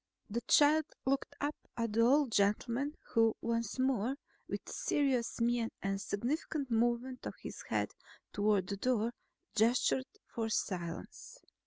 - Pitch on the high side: Yes, high, 235 Hz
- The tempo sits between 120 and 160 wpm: Yes, average, 140 wpm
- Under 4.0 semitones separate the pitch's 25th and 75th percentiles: Yes, average, 3.6 semitones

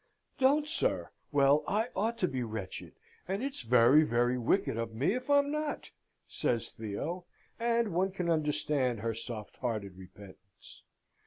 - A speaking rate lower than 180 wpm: Yes, average, 150 wpm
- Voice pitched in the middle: Yes, medium, 145 Hz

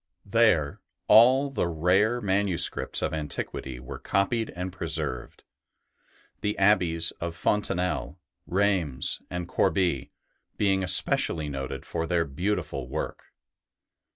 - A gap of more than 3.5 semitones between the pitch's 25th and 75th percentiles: Yes, average, 4.5 semitones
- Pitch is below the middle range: Yes, very low, 90 Hz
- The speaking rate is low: Yes, slow, 105 wpm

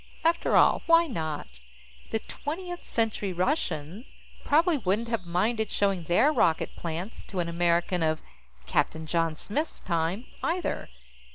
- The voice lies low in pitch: No, high, 190 Hz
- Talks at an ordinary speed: No, slow, 130 wpm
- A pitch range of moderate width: No, wide, 7.7 semitones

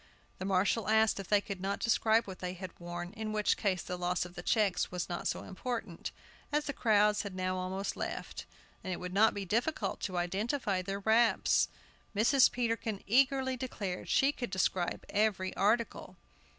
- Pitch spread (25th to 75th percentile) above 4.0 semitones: No, average, 3.6 semitones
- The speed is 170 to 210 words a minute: Yes, average, 180 wpm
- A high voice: Yes, high, 200 Hz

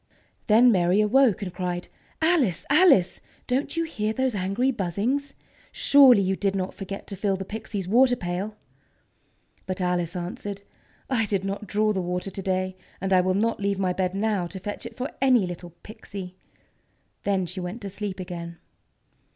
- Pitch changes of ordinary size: Yes, average, 3.4 semitones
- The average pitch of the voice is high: Yes, high, 195 Hz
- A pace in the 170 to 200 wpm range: Yes, average, 175 wpm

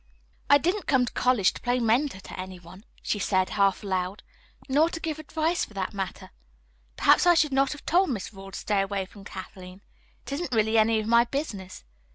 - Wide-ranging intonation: Yes, wide, 6.5 semitones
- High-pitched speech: Yes, high, 220 Hz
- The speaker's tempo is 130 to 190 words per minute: No, fast, 205 wpm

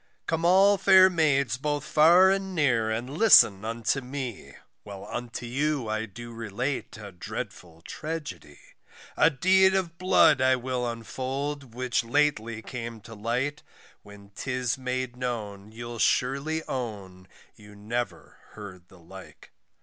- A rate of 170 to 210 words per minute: No, slow, 135 wpm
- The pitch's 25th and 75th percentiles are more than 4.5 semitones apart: Yes, average, 5.3 semitones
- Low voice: Yes, low, 125 Hz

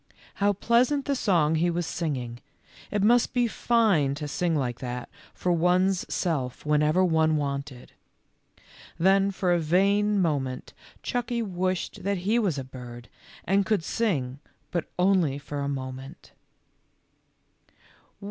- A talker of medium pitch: Yes, medium, 170 Hz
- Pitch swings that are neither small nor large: No, wide, 6.0 semitones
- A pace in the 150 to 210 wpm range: No, slow, 135 wpm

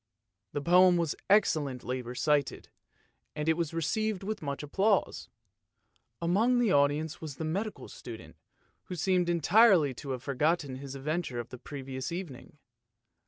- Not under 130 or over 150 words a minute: Yes, average, 140 wpm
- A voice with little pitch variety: No, average, 4.6 semitones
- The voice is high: No, medium, 155 Hz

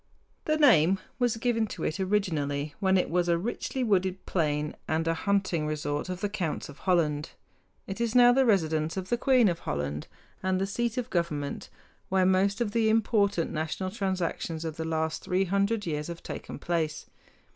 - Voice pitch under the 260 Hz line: Yes, medium, 185 Hz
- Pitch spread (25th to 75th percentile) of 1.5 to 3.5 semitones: No, average, 4.5 semitones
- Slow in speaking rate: No, average, 185 wpm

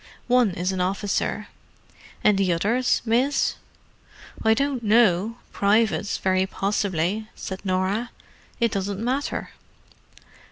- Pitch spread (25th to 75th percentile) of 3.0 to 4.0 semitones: Yes, average, 3.6 semitones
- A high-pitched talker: Yes, high, 205 Hz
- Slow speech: Yes, slow, 105 wpm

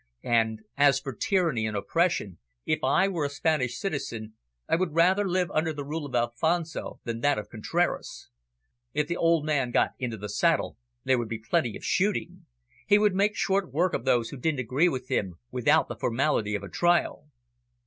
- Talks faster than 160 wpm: Yes, average, 190 wpm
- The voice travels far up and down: Yes, wide, 6.5 semitones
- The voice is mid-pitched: Yes, medium, 145 Hz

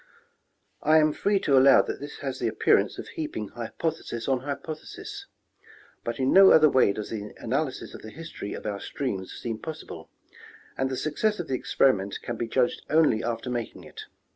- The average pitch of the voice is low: Yes, low, 130 Hz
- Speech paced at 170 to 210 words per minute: Yes, average, 185 wpm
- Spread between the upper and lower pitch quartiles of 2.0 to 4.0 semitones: No, average, 5.2 semitones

